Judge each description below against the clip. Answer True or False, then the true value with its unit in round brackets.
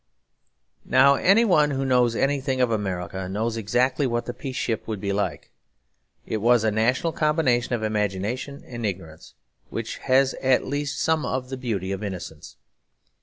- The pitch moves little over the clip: False (4.5 semitones)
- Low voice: True (120 Hz)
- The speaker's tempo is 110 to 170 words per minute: True (165 wpm)